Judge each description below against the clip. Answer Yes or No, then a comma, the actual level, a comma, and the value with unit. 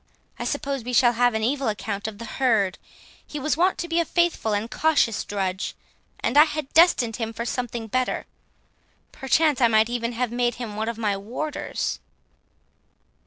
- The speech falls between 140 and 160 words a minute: No, average, 180 wpm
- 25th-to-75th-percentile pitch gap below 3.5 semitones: No, average, 4.1 semitones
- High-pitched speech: Yes, high, 240 Hz